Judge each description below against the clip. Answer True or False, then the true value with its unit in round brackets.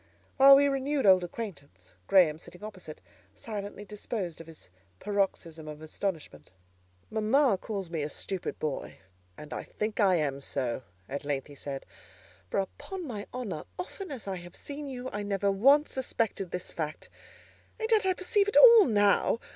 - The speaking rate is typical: True (165 wpm)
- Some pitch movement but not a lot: False (8.2 semitones)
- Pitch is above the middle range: True (200 Hz)